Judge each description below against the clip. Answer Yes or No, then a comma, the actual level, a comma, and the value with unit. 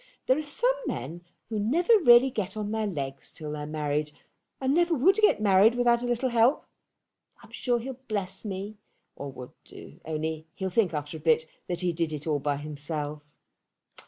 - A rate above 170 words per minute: Yes, average, 190 wpm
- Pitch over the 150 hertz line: Yes, high, 190 Hz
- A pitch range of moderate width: No, wide, 8.0 semitones